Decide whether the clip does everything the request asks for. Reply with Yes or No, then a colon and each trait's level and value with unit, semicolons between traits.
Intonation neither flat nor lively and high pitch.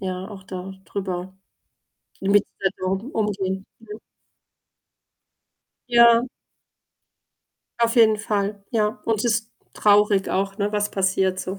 No: narrow, 2.3 semitones; high, 200 Hz